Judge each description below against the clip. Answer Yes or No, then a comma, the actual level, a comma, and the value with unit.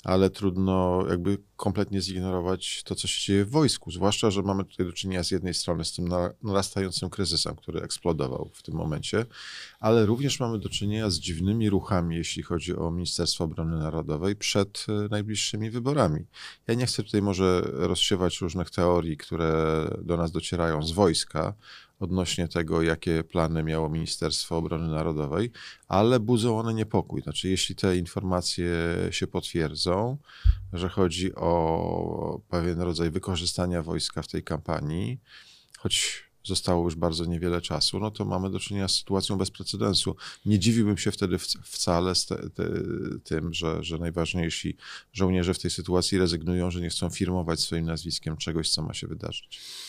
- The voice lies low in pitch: Yes, very low, 90 Hz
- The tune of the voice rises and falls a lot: No, average, 2.9 semitones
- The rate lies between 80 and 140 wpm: No, fast, 160 wpm